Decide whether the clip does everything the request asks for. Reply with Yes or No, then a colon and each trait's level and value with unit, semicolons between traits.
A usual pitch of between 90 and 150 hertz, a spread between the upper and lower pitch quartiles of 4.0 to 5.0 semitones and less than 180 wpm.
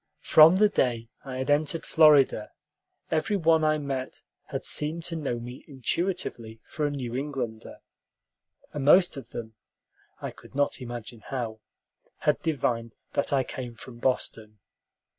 Yes: low, 135 Hz; average, 4.4 semitones; average, 145 wpm